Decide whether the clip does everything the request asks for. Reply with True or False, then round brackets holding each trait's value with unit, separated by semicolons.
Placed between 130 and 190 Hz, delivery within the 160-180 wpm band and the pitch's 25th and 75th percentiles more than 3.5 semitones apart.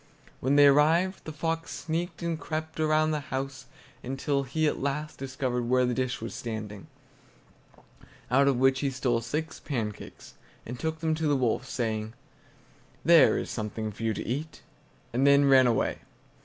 True (135 Hz; 170 wpm; 4.2 semitones)